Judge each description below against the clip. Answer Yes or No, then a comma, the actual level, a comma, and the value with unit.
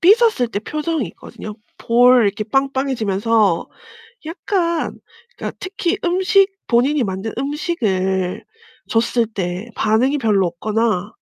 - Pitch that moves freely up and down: Yes, wide, 6.7 semitones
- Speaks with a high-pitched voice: Yes, high, 235 Hz